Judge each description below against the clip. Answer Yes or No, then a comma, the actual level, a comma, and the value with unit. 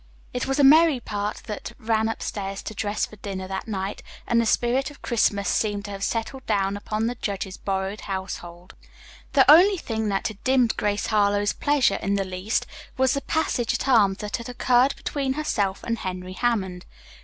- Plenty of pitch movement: No, average, 4.1 semitones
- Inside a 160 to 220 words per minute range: Yes, average, 190 wpm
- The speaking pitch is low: No, high, 215 Hz